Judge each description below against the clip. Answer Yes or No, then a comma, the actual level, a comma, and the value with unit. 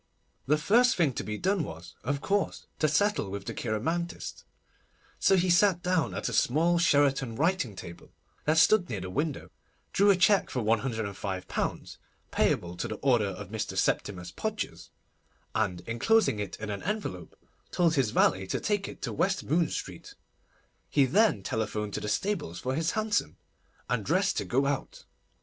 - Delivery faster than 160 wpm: Yes, average, 170 wpm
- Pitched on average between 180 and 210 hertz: No, medium, 140 Hz